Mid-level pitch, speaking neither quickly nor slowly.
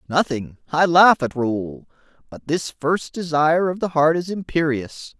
Yes: medium, 155 Hz; average, 150 wpm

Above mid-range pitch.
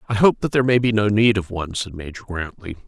No: low, 105 Hz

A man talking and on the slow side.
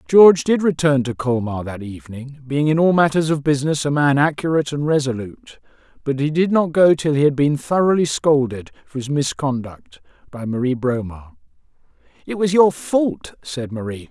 No: male; average, 175 wpm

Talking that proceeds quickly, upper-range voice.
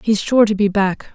Yes: fast, 260 wpm; high, 205 Hz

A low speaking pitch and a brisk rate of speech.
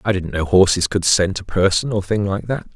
Yes: low, 100 Hz; fast, 260 wpm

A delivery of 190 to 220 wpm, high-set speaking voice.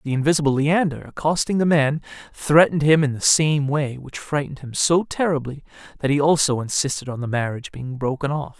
No: average, 195 wpm; medium, 145 Hz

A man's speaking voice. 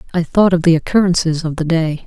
No: female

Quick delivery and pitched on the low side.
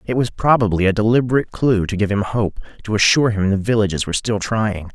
Yes: fast, 220 wpm; low, 105 Hz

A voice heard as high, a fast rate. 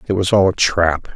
No: very low, 90 Hz; fast, 260 wpm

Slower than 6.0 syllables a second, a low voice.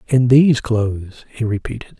Yes: 5.5 syllables/s; low, 120 Hz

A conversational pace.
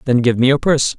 No: fast, 305 wpm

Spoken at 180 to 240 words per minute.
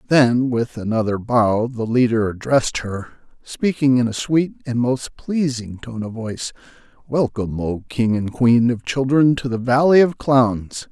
No: average, 165 wpm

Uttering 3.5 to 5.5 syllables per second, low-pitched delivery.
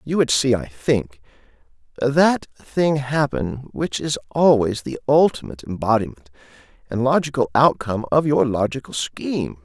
Yes: 4.7 syllables/s; low, 120 Hz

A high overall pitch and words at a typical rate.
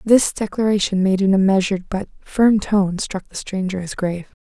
Yes: high, 195 Hz; average, 190 wpm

